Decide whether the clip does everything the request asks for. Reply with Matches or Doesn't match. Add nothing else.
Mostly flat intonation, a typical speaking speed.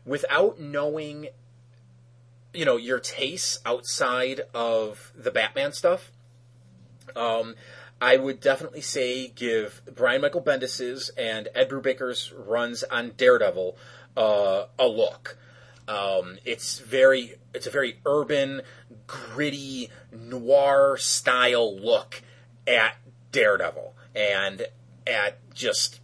Doesn't match